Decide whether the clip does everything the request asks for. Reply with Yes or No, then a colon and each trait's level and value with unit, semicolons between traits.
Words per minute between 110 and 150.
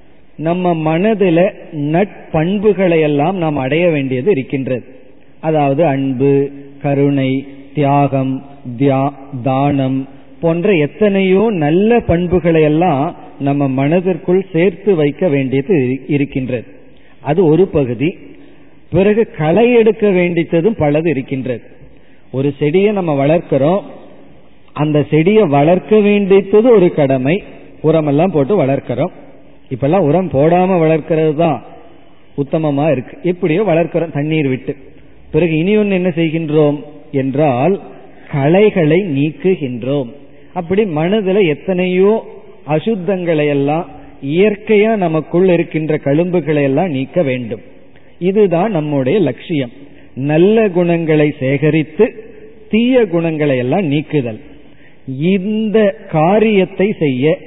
No: average, 95 wpm